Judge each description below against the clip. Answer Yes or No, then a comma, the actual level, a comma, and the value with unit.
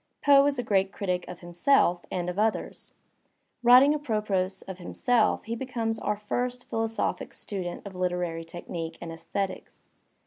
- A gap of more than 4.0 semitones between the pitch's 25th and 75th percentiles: Yes, average, 5.1 semitones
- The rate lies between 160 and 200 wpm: No, average, 145 wpm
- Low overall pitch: No, high, 200 Hz